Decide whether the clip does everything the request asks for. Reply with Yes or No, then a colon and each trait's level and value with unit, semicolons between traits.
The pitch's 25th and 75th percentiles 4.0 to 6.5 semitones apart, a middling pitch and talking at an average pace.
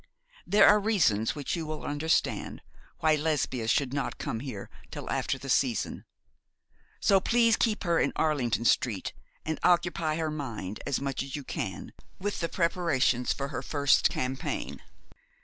Yes: average, 4.7 semitones; medium, 145 Hz; average, 155 wpm